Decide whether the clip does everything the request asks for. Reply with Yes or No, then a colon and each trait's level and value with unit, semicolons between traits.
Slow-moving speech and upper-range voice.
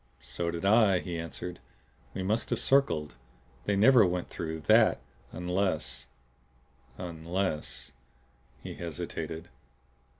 No: slow, 110 wpm; very low, 85 Hz